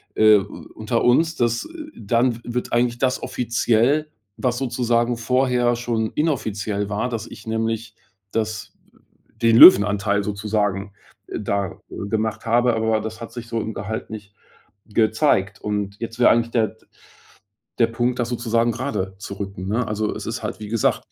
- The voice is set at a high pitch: No, low, 115 Hz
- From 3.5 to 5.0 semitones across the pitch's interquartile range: No, narrow, 2.4 semitones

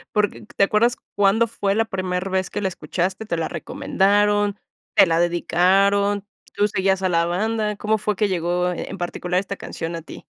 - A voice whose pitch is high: Yes, high, 195 Hz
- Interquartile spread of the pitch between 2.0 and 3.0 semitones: Yes, narrow, 2.6 semitones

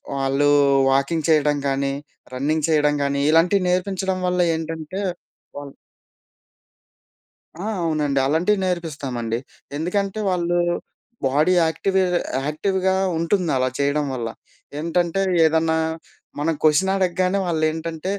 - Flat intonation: No, average, 3.8 semitones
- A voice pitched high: No, medium, 160 Hz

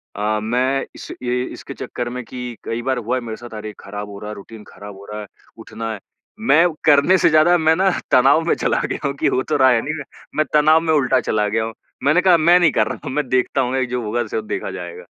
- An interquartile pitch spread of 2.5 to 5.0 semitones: No, wide, 5.6 semitones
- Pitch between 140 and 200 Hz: No, low, 125 Hz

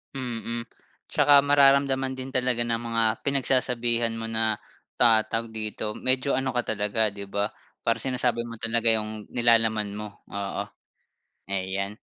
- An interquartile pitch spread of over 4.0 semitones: No, average, 2.8 semitones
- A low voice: Yes, low, 115 Hz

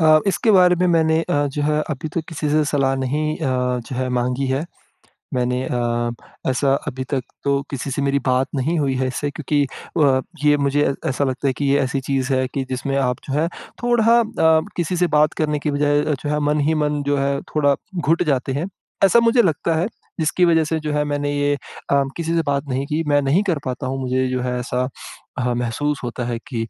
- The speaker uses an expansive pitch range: No, average, 2.9 semitones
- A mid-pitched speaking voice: Yes, medium, 145 Hz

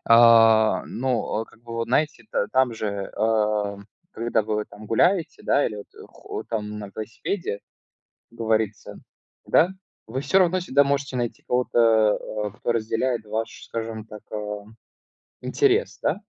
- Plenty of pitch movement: No, average, 3.1 semitones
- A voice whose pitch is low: Yes, low, 115 Hz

